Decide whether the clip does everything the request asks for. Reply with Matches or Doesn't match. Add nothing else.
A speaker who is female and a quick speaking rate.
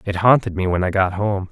Doesn't match